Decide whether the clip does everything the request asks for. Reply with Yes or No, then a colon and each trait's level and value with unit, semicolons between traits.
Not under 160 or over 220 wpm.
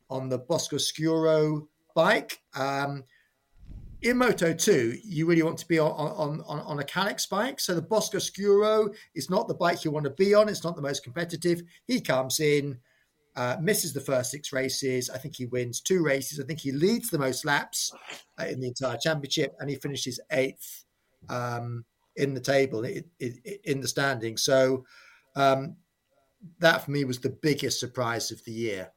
Yes: average, 190 wpm